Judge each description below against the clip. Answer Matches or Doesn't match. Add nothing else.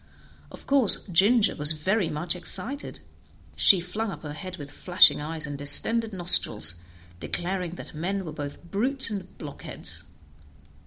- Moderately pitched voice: Matches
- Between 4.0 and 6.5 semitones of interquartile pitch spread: Matches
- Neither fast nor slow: Matches